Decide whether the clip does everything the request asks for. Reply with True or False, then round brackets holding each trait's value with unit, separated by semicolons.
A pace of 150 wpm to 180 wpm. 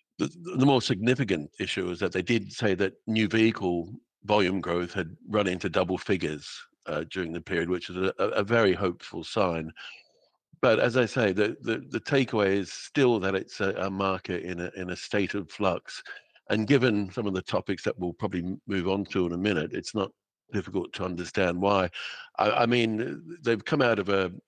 False (200 wpm)